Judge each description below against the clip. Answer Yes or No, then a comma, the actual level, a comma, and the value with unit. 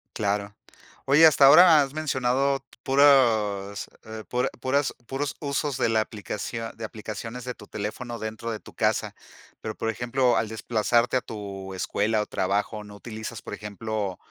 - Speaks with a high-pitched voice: No, low, 115 Hz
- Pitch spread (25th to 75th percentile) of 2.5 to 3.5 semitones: No, average, 3.9 semitones